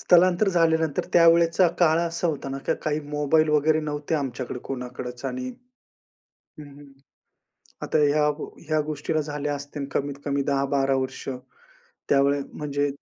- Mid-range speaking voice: Yes, medium, 150 Hz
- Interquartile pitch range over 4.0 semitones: No, average, 2.7 semitones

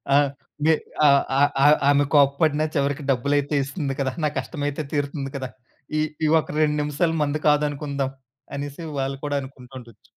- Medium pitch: Yes, medium, 145 Hz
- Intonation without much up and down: Yes, narrow, 1.3 semitones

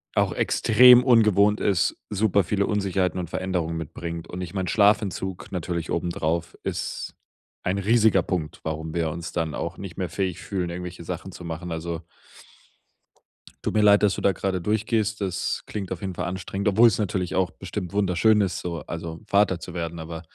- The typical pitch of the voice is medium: No, very low, 90 Hz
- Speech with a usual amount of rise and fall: Yes, average, 3.1 semitones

